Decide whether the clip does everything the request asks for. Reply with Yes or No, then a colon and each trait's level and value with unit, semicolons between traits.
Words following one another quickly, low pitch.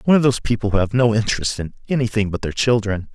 Yes: fast, 250 wpm; low, 110 Hz